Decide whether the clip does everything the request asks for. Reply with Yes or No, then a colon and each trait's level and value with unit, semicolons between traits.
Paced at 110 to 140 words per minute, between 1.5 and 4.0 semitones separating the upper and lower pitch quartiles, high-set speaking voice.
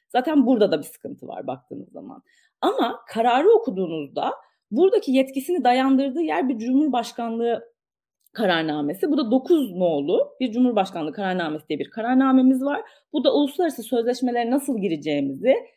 No: average, 135 wpm; average, 4.4 semitones; very high, 260 Hz